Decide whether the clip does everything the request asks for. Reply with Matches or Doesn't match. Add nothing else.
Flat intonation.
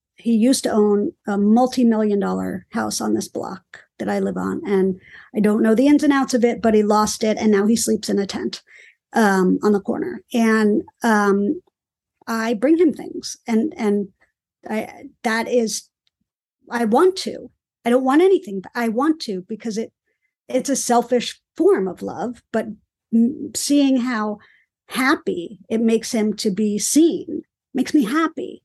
Doesn't match